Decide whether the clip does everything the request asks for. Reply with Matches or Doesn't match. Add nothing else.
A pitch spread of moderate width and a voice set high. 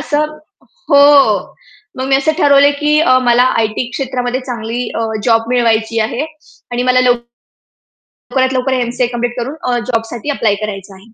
Matches